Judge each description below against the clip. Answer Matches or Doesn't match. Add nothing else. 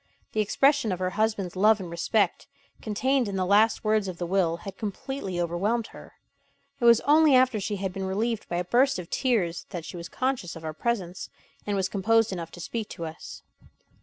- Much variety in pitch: Doesn't match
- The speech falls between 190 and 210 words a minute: Matches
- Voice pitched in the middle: Doesn't match